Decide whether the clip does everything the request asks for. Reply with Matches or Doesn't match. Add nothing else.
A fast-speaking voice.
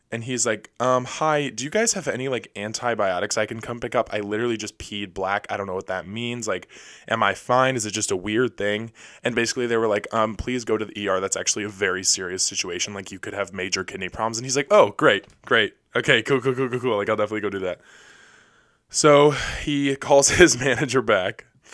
Matches